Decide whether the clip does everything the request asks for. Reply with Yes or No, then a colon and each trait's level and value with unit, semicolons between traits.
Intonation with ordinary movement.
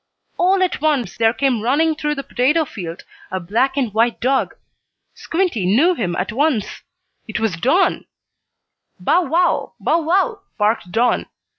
No: wide, 6.7 semitones